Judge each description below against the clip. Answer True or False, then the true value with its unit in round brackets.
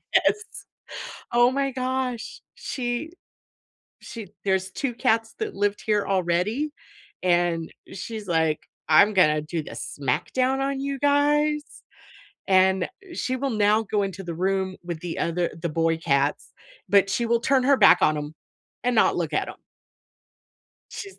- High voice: True (205 Hz)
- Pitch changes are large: True (6.9 semitones)